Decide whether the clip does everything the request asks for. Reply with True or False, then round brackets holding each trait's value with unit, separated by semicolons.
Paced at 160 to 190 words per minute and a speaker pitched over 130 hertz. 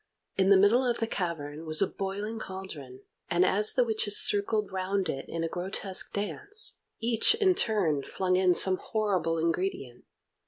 True (165 wpm; 190 Hz)